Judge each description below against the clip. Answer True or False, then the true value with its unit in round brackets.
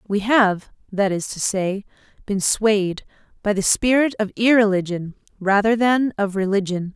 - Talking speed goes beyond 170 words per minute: False (145 wpm)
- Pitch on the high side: True (205 Hz)